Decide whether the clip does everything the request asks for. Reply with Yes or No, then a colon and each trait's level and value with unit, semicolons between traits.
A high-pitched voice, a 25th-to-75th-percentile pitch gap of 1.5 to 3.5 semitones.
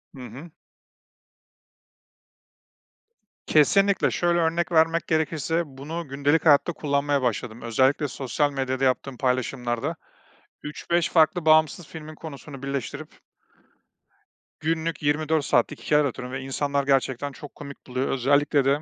No: medium, 145 Hz; average, 2.8 semitones